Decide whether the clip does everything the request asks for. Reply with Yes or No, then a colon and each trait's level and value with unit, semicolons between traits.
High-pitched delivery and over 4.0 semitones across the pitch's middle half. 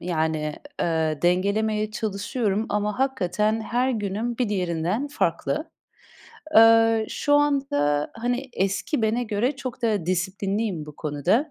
Yes: high, 210 Hz; average, 4.9 semitones